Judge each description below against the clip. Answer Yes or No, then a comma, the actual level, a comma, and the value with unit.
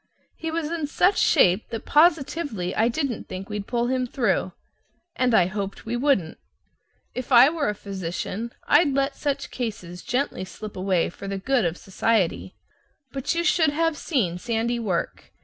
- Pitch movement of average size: No, wide, 6.5 semitones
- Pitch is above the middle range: Yes, high, 235 Hz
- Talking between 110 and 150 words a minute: No, average, 165 wpm